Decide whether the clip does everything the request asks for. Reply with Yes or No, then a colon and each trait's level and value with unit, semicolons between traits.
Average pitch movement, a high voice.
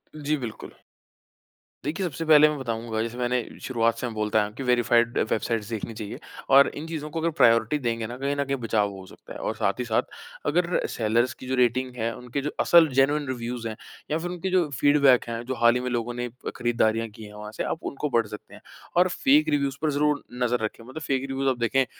No: average, 4.0 semitones; low, 125 Hz